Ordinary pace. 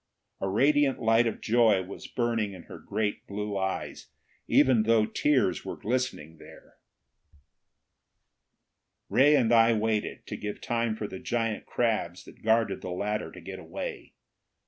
Yes: average, 145 wpm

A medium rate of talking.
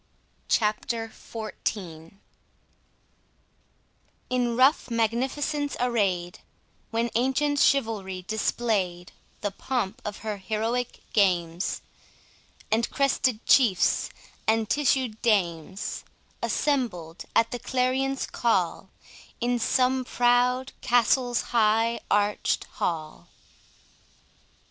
No: slow, 85 wpm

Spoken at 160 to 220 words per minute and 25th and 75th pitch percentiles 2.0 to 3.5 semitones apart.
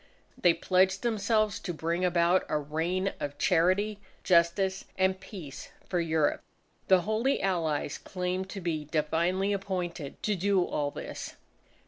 No: slow, 135 wpm; average, 2.7 semitones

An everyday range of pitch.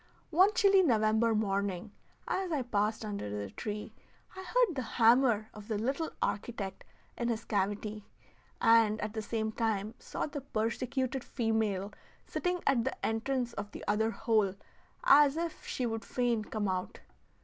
Yes: average, 3.7 semitones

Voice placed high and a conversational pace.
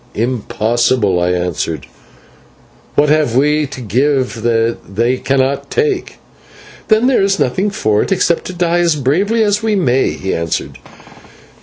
No: low, 135 Hz; average, 145 wpm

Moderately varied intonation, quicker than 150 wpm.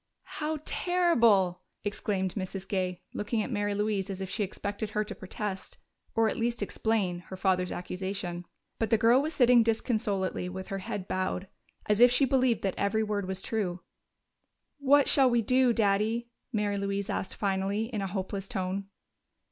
Yes: average, 3.2 semitones; average, 170 wpm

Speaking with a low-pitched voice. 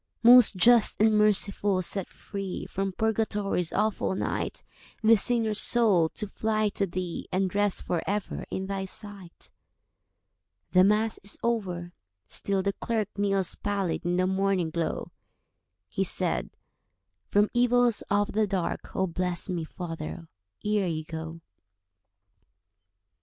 No: high, 195 Hz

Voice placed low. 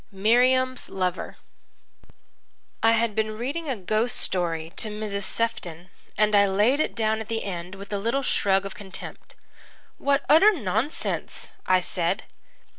No: high, 215 Hz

